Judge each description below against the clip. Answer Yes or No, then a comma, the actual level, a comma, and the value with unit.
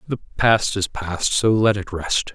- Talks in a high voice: No, low, 105 Hz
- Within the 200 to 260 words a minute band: Yes, fast, 205 wpm